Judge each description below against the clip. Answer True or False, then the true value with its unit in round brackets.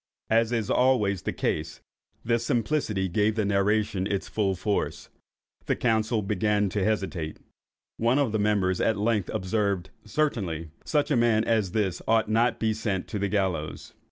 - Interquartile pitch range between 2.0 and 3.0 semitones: True (2.6 semitones)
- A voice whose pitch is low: True (105 Hz)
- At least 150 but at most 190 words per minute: True (160 wpm)